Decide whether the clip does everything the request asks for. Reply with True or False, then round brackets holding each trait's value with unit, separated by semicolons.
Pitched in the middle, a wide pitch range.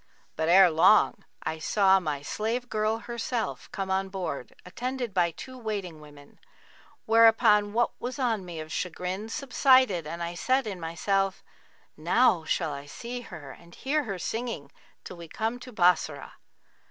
False (195 Hz; 5.7 semitones)